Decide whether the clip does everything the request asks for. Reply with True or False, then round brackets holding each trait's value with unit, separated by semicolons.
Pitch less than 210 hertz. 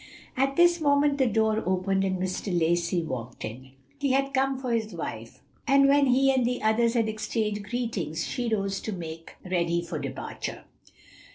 False (220 Hz)